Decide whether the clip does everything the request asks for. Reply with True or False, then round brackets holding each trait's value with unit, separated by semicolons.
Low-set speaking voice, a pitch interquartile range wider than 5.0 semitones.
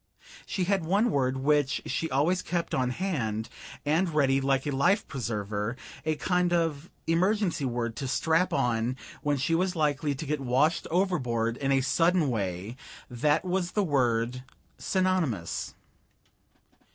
False (145 Hz; 5.5 semitones)